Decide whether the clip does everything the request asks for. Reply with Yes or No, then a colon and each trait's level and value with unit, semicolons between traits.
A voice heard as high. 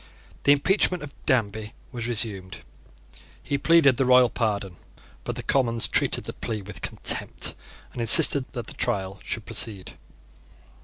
No: low, 115 Hz